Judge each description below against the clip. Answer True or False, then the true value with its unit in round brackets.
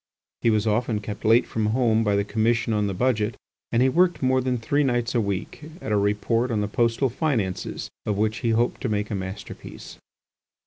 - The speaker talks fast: True (210 wpm)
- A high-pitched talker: False (115 Hz)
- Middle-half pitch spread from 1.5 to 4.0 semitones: True (2.8 semitones)